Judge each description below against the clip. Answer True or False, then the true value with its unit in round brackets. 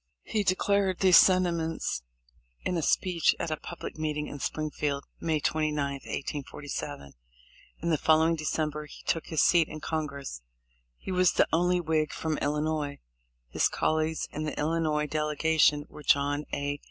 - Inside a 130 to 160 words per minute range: True (155 wpm)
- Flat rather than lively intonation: True (1.8 semitones)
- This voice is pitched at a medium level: True (155 Hz)